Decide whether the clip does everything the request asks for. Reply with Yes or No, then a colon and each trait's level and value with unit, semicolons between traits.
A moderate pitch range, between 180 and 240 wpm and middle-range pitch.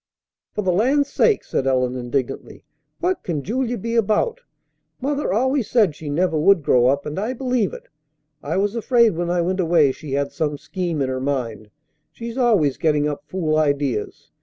No: wide, 8.4 semitones; average, 185 wpm; medium, 175 Hz